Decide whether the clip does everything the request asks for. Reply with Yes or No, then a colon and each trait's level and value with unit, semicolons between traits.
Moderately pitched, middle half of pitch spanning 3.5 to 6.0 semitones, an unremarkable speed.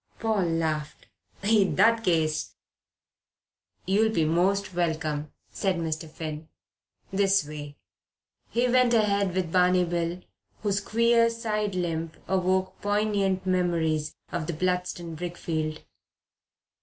No: medium, 180 Hz; average, 3.8 semitones; slow, 115 wpm